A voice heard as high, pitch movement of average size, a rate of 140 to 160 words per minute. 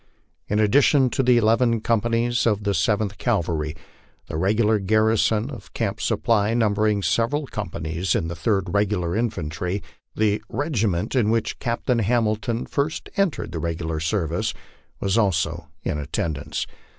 No: low, 105 Hz; average, 4.6 semitones; average, 145 wpm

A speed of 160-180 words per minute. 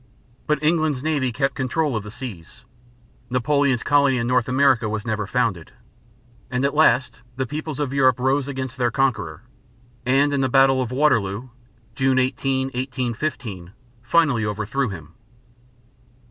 No: average, 145 wpm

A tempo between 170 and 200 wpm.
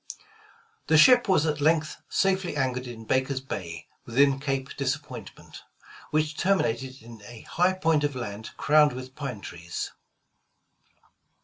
No: slow, 135 wpm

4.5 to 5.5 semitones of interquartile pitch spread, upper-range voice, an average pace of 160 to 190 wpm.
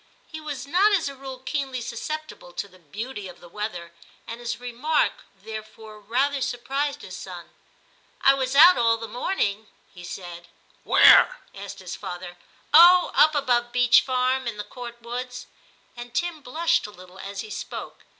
Yes: average, 4.9 semitones; high, 245 Hz; average, 180 wpm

